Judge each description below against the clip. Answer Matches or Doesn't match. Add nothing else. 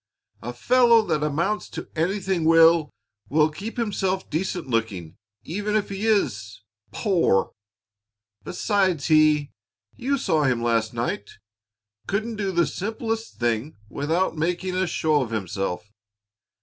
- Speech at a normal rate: Doesn't match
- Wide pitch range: Matches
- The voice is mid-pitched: Matches